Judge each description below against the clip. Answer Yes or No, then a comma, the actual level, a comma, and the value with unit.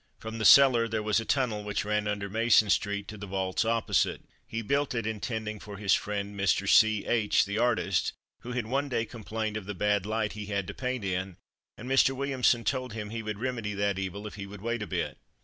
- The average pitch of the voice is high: No, low, 105 Hz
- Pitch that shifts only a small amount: Yes, narrow, 2.2 semitones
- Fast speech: Yes, fast, 230 wpm